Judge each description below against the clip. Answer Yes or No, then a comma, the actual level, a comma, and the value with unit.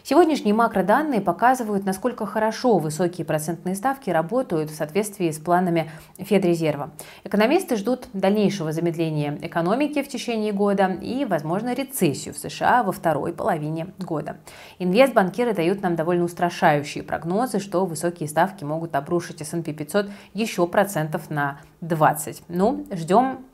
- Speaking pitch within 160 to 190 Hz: Yes, medium, 185 Hz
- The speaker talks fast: No, average, 125 wpm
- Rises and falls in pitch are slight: No, average, 4.7 semitones